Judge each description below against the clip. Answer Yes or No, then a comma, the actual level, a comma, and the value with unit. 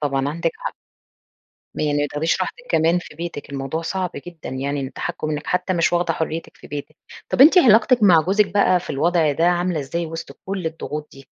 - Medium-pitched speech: Yes, medium, 165 Hz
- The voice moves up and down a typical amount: Yes, average, 3.5 semitones